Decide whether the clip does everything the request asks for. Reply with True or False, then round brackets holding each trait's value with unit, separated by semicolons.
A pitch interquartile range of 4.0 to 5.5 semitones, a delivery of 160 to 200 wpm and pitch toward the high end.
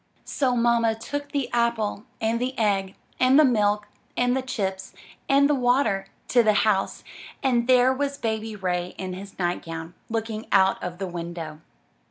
True (4.5 semitones; 165 wpm; 220 Hz)